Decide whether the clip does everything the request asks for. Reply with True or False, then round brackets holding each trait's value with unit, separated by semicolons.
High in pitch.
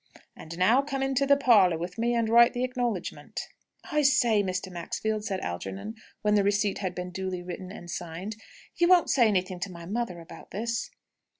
True (205 Hz)